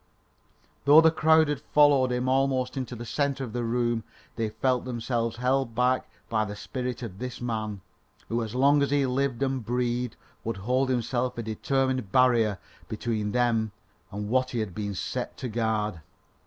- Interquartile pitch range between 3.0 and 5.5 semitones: No, narrow, 2.6 semitones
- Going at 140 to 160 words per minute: No, average, 175 wpm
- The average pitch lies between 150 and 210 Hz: No, low, 125 Hz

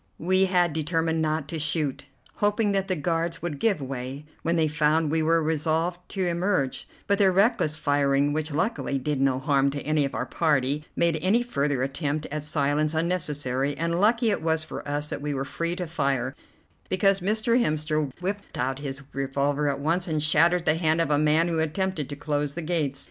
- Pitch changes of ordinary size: Yes, average, 3.2 semitones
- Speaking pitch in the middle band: Yes, medium, 155 Hz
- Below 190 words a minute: No, average, 195 wpm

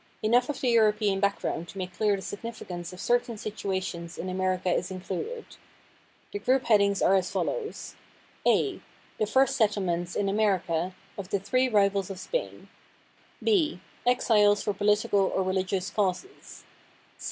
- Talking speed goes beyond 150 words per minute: No, average, 145 wpm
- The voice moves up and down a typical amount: Yes, average, 3.4 semitones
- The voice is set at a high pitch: Yes, high, 200 Hz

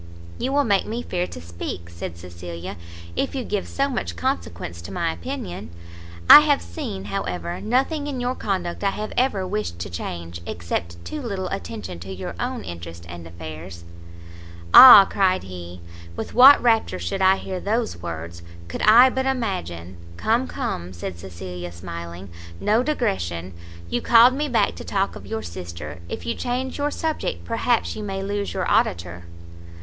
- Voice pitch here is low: Yes, very low, 95 Hz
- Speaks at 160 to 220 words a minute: Yes, average, 170 wpm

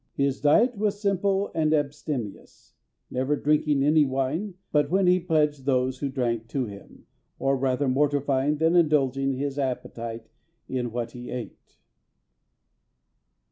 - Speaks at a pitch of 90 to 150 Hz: Yes, medium, 140 Hz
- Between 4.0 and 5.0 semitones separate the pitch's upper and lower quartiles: No, average, 3.0 semitones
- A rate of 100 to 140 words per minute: Yes, slow, 135 wpm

